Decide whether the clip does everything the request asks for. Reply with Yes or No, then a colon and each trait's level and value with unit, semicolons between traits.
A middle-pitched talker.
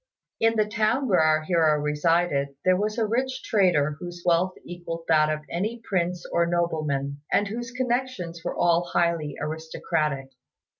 Yes: medium, 170 Hz